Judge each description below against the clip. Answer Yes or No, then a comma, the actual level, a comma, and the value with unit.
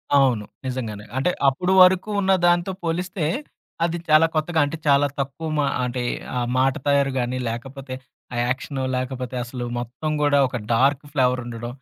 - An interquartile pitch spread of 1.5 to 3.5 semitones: No, average, 3.9 semitones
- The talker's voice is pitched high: No, low, 135 Hz